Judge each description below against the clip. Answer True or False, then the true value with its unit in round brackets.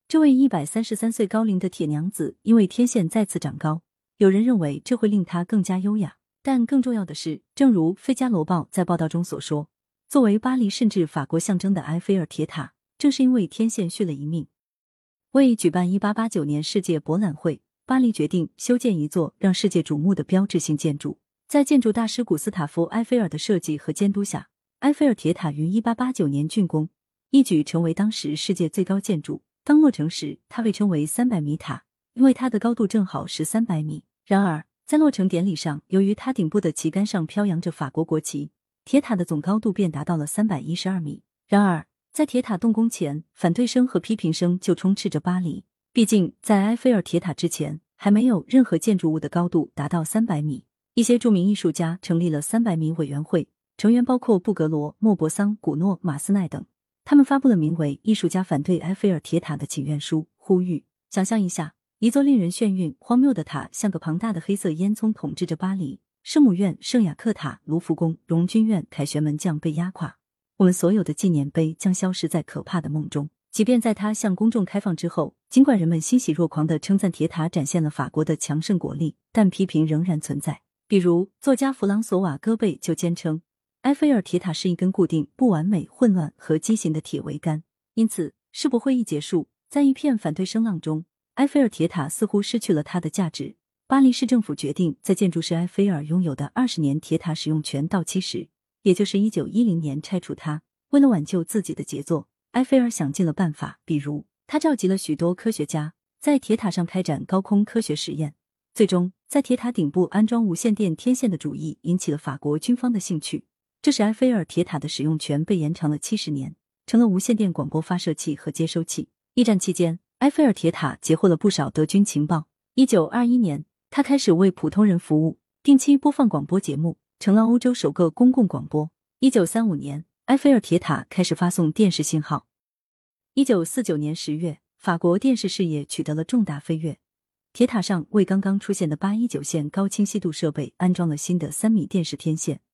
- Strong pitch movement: True (5.7 semitones)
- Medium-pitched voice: True (180 Hz)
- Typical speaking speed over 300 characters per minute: True (315 characters per minute)